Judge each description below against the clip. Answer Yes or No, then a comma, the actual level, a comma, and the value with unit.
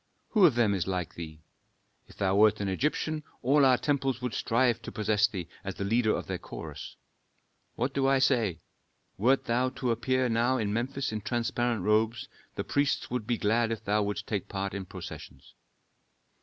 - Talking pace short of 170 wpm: No, average, 185 wpm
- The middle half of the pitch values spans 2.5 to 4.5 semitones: Yes, average, 4.0 semitones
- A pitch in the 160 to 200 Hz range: No, low, 115 Hz